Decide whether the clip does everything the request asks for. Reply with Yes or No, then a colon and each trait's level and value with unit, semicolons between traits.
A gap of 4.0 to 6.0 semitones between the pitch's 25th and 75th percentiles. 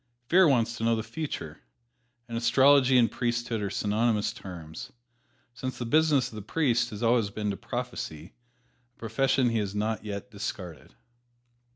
No: average, 3.4 semitones